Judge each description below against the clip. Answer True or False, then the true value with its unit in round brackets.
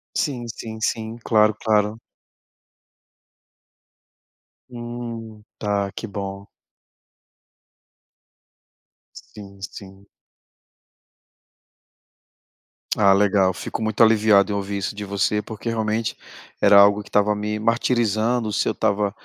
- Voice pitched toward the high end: False (105 Hz)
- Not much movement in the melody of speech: True (1.9 semitones)